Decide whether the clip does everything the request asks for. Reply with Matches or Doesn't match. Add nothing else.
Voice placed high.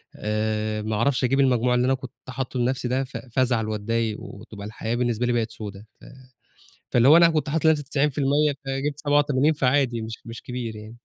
Doesn't match